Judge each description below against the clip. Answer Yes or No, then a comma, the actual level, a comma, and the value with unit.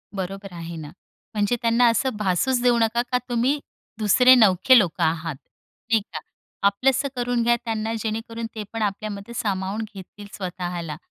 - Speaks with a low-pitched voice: No, high, 215 Hz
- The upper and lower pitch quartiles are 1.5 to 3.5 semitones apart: No, average, 4.0 semitones